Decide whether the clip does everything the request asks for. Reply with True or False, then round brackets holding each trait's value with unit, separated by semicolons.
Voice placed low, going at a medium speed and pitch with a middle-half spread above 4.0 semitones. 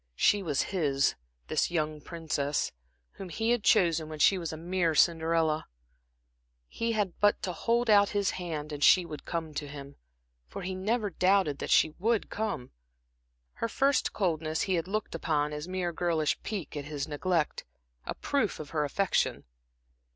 False (170 Hz; 170 wpm; 4.5 semitones)